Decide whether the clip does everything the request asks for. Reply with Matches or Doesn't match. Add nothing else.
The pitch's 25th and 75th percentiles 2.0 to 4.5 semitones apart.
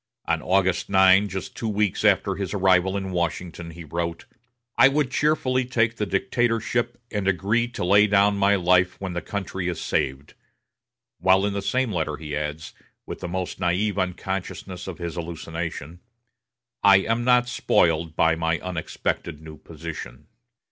Matches